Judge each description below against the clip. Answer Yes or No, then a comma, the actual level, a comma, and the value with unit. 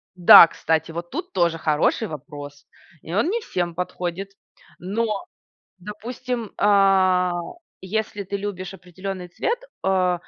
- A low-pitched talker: No, medium, 185 Hz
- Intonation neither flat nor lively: Yes, average, 3.0 semitones